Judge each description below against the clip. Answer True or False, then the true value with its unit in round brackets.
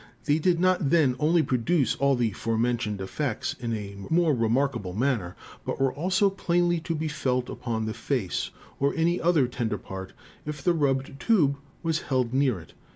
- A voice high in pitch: False (135 Hz)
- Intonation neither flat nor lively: False (5.7 semitones)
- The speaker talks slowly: False (180 wpm)